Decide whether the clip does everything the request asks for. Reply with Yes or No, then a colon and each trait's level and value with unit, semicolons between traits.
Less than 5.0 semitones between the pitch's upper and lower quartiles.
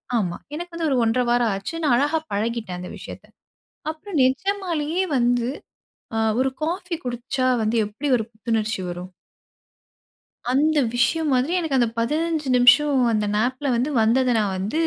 No: wide, 5.4 semitones